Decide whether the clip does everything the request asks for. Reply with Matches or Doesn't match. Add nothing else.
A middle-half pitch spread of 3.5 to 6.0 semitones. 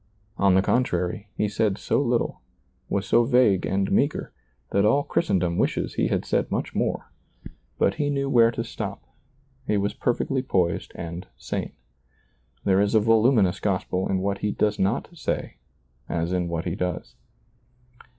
Matches